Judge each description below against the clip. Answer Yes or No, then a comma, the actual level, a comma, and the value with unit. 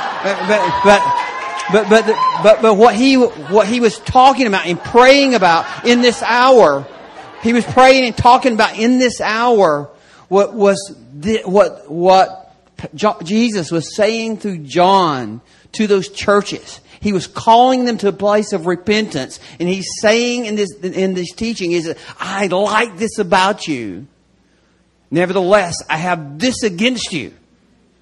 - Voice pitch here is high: Yes, high, 205 Hz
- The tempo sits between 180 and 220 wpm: No, average, 150 wpm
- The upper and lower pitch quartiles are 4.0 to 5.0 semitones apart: Yes, average, 4.4 semitones